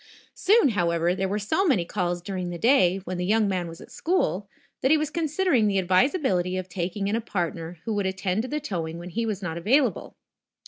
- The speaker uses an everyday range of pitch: No, wide, 5.7 semitones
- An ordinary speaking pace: No, fast, 220 wpm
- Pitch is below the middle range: No, high, 195 Hz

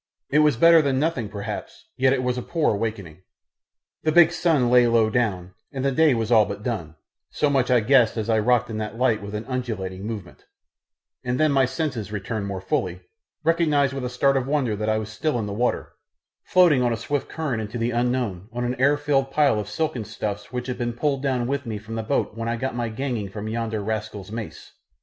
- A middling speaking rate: No, fast, 230 wpm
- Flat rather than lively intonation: No, average, 4.0 semitones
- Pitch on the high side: No, low, 120 Hz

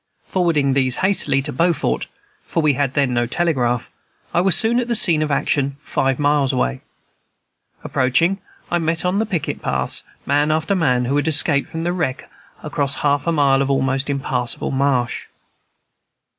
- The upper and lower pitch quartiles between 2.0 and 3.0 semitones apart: No, average, 3.8 semitones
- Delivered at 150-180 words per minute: Yes, average, 170 wpm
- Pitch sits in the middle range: Yes, medium, 145 Hz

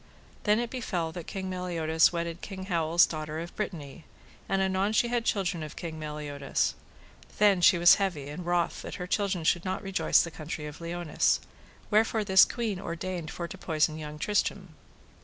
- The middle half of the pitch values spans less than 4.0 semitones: Yes, average, 3.3 semitones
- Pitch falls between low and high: Yes, medium, 175 Hz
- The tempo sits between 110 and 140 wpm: No, average, 175 wpm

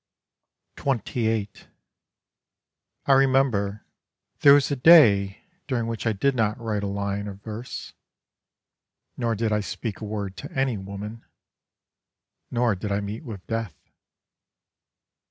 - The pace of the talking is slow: Yes, slow, 125 wpm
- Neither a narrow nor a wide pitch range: Yes, average, 3.5 semitones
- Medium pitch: No, low, 110 Hz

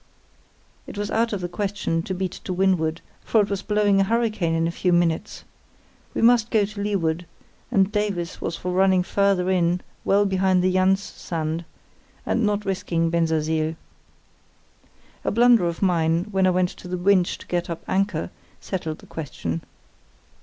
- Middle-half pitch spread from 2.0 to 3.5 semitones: Yes, average, 3.1 semitones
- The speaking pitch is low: No, medium, 185 Hz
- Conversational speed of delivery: Yes, average, 170 wpm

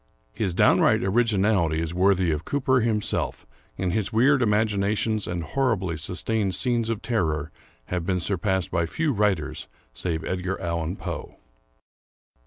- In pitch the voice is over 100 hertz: No, very low, 95 Hz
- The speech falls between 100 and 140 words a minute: Yes, slow, 135 wpm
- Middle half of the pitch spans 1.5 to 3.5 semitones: No, average, 4.3 semitones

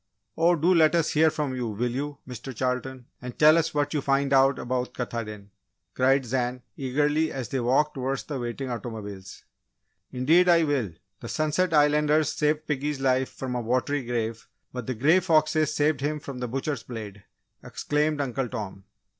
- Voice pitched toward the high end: No, low, 135 Hz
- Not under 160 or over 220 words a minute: Yes, average, 175 wpm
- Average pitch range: Yes, average, 3.5 semitones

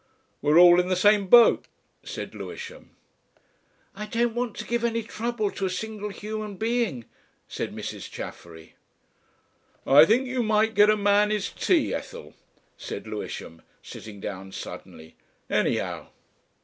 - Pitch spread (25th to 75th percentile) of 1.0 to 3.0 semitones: No, average, 4.3 semitones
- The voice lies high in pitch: Yes, high, 210 Hz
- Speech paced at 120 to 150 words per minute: Yes, average, 140 wpm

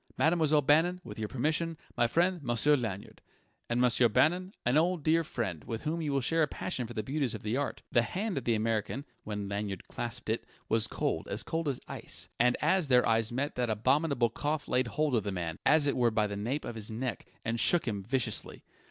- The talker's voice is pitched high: No, low, 125 Hz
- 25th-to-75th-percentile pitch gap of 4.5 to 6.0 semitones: Yes, wide, 5.5 semitones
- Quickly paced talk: Yes, fast, 220 wpm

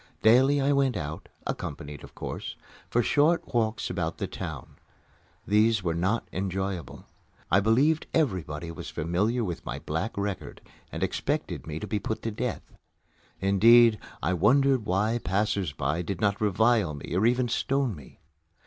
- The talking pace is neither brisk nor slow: Yes, average, 150 wpm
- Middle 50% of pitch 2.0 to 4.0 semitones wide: No, average, 5.2 semitones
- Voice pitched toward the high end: No, low, 105 Hz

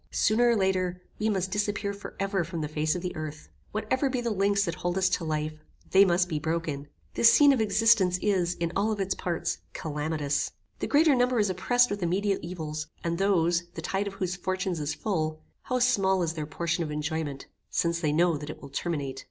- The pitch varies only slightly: No, average, 4.2 semitones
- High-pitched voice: No, medium, 180 Hz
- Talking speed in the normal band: No, fast, 210 wpm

